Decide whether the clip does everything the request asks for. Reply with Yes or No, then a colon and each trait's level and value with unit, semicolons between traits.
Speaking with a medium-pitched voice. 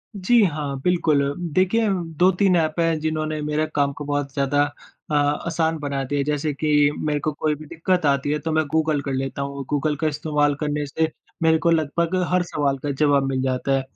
Yes: medium, 150 Hz